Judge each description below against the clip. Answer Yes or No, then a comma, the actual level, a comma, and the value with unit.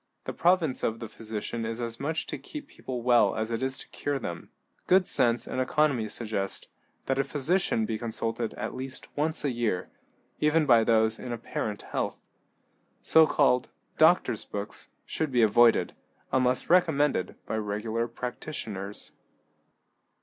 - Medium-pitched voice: No, low, 120 Hz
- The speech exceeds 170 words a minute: No, average, 150 wpm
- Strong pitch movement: No, average, 4.5 semitones